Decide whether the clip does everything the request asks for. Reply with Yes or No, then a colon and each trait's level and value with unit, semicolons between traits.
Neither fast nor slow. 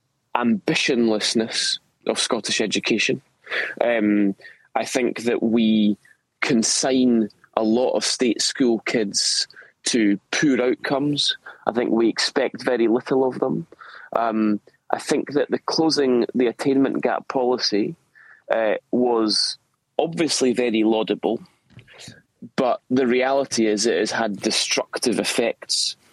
No: slow, 115 wpm